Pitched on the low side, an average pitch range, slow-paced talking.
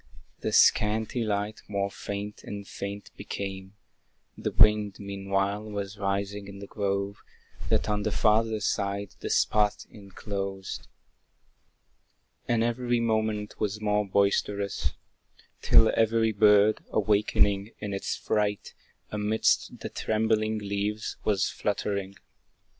No: low, 105 Hz; narrow, 1.3 semitones; slow, 115 wpm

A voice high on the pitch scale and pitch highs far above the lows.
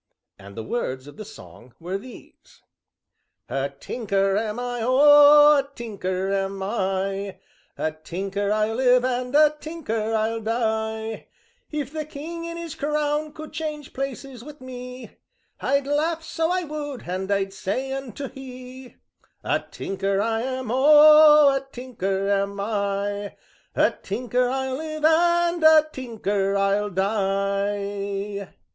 Yes: high, 240 Hz; wide, 6.6 semitones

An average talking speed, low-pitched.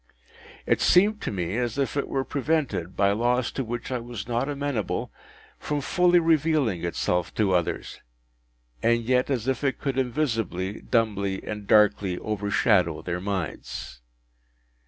Yes: average, 145 wpm; low, 115 Hz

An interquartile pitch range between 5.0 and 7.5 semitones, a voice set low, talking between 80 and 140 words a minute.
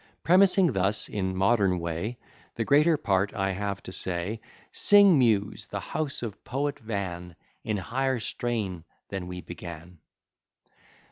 Yes: wide, 5.5 semitones; low, 100 Hz; slow, 135 wpm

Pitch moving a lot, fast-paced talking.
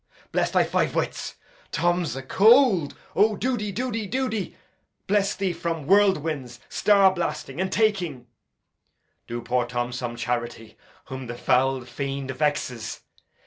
No: wide, 8.2 semitones; average, 145 wpm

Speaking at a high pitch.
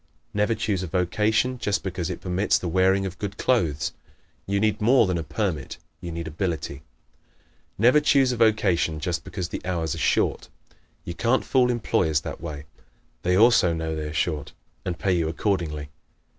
No: very low, 90 Hz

